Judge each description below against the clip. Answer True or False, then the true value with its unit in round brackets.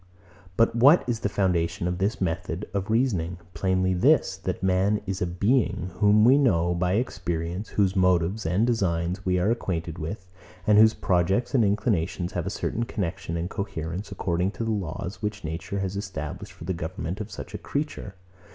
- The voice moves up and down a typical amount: True (3.4 semitones)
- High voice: False (95 Hz)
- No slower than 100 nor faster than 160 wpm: False (180 wpm)